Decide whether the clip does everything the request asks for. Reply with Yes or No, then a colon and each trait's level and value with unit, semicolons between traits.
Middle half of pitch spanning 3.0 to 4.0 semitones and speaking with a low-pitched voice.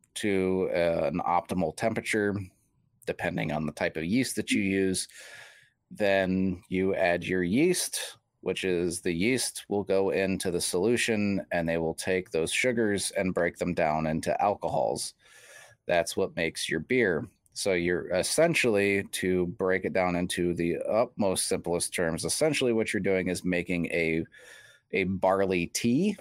No: narrow, 2.4 semitones; very low, 95 Hz